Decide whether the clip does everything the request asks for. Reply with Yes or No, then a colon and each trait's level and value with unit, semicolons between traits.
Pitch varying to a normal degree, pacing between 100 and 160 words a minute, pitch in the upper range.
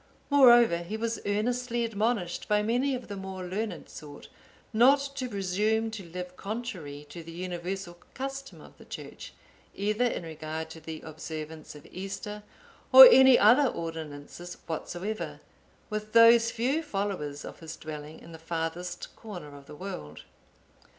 No: wide, 5.9 semitones; average, 150 wpm; high, 195 Hz